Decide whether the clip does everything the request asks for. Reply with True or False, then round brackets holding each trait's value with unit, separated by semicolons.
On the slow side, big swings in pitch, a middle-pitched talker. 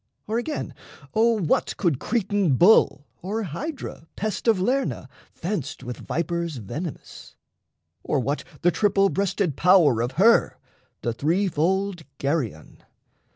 True (125 wpm; 5.8 semitones; 180 Hz)